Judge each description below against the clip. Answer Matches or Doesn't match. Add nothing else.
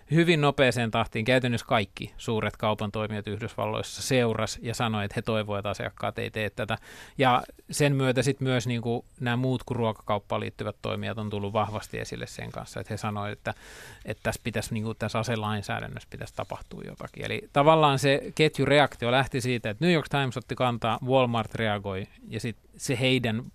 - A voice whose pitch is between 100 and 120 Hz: Matches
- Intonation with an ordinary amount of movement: Matches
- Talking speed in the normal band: Doesn't match